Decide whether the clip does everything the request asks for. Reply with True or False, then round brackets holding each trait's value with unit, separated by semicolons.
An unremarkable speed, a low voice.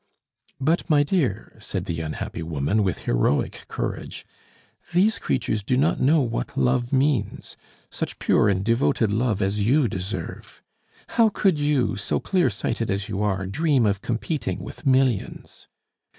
True (150 wpm; 115 Hz)